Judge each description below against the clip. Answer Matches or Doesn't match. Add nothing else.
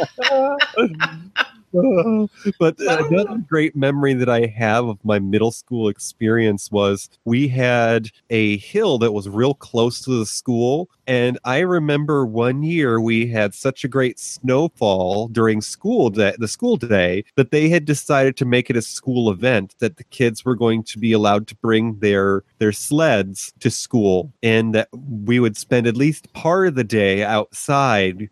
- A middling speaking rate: Matches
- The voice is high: Doesn't match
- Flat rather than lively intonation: Doesn't match